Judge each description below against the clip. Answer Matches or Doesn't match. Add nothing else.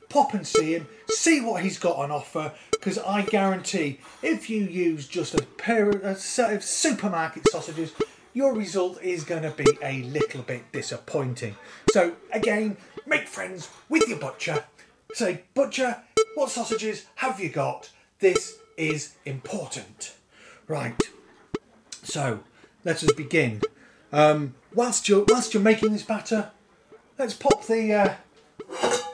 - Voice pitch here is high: Matches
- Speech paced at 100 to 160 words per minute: Matches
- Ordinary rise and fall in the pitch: Doesn't match